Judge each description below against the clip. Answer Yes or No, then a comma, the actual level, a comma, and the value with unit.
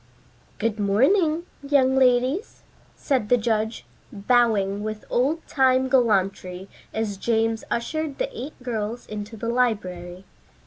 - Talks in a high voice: Yes, high, 235 Hz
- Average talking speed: No, slow, 120 wpm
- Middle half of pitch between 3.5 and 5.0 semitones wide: Yes, average, 4.0 semitones